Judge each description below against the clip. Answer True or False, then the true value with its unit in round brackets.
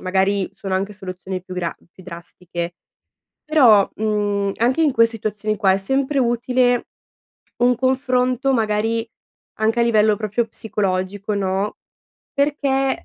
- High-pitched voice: True (215 Hz)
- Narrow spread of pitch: False (4.3 semitones)